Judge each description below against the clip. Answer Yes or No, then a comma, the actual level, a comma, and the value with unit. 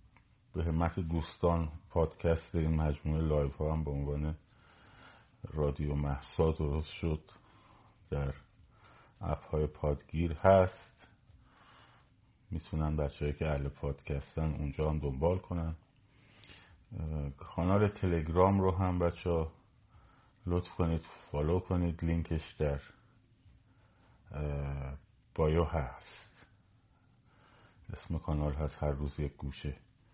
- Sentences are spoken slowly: Yes, slow, 100 wpm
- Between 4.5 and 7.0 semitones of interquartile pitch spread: No, average, 4.1 semitones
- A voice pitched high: No, very low, 80 Hz